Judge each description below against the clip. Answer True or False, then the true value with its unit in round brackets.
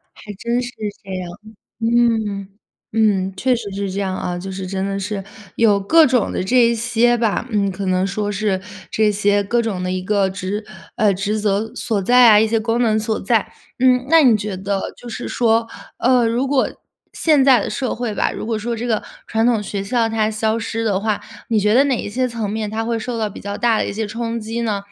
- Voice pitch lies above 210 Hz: True (220 Hz)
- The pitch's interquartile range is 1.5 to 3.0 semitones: True (2.7 semitones)